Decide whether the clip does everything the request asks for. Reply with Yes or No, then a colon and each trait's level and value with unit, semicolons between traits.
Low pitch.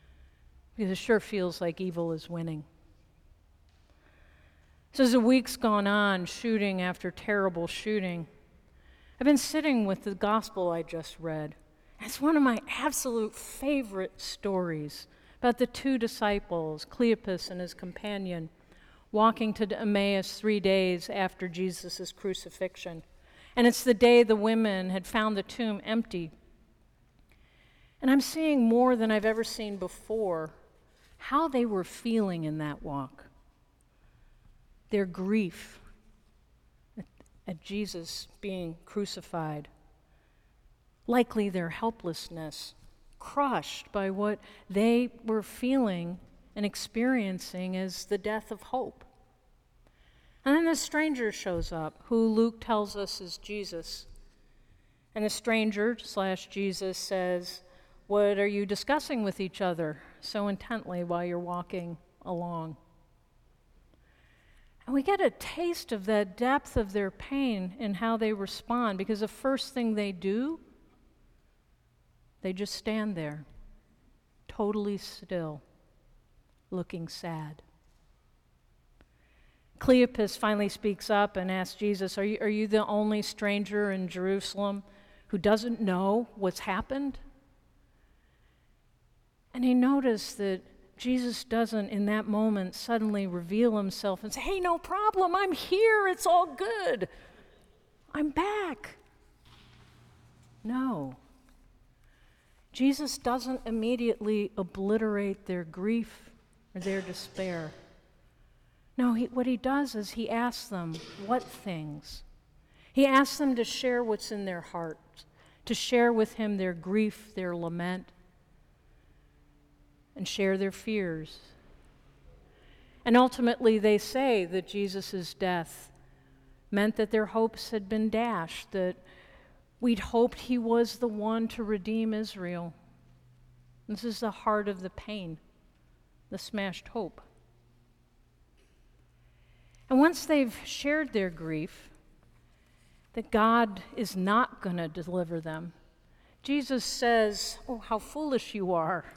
No: high, 205 Hz